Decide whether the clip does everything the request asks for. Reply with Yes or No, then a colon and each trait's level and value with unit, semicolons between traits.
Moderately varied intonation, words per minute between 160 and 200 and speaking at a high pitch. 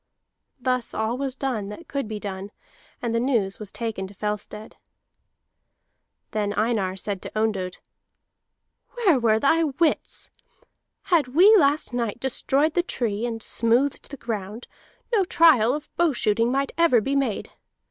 No: average, 4.7 semitones; average, 145 wpm; high, 235 Hz